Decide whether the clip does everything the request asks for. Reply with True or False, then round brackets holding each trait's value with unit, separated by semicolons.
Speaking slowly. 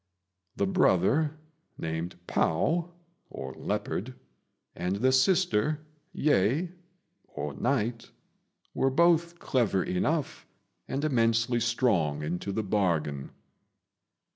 True (85 wpm)